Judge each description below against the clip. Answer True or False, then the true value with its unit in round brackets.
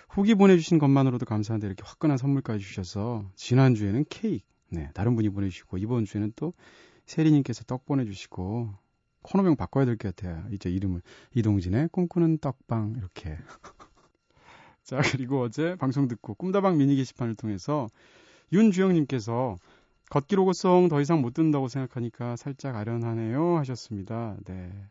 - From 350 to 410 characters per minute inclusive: True (360 characters per minute)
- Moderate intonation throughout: False (5.7 semitones)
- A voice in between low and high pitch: False (125 Hz)